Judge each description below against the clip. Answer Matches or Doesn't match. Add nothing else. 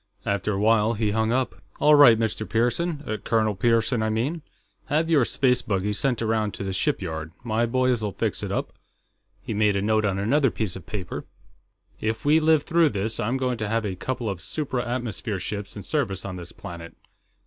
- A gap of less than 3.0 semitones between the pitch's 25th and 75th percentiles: Doesn't match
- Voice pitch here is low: Matches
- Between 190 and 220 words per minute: Matches